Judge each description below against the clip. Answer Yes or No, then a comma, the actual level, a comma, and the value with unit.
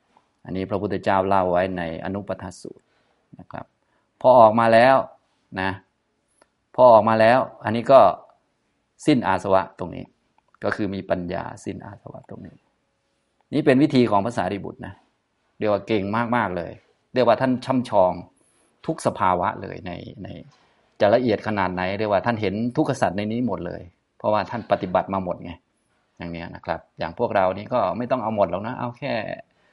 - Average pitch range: Yes, average, 3.4 semitones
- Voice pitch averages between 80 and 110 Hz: Yes, low, 100 Hz